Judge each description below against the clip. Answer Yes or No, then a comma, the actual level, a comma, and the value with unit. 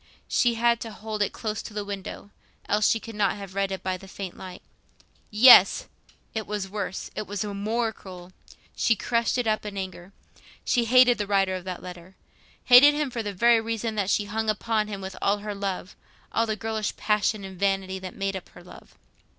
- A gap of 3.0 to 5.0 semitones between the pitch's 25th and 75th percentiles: No, narrow, 2.6 semitones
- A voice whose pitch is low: No, high, 205 Hz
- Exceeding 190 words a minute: Yes, average, 200 wpm